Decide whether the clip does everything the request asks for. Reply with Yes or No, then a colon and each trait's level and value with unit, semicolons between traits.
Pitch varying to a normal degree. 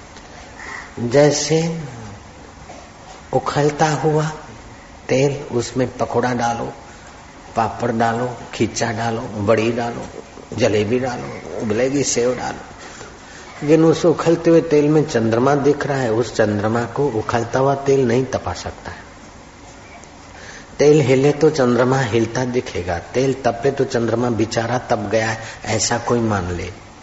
Yes: average, 3.8 semitones